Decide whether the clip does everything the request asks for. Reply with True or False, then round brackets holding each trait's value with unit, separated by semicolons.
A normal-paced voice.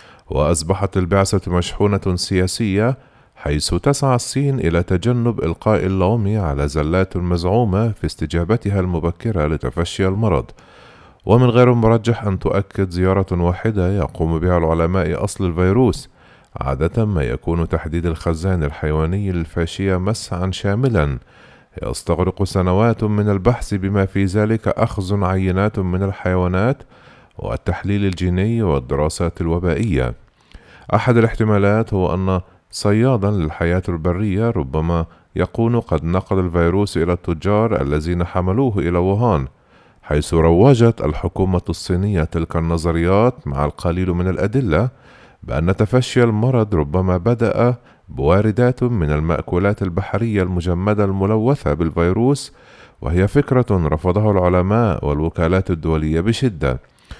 True (105 wpm)